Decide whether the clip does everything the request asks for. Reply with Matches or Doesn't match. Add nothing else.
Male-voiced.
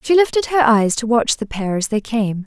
Doesn't match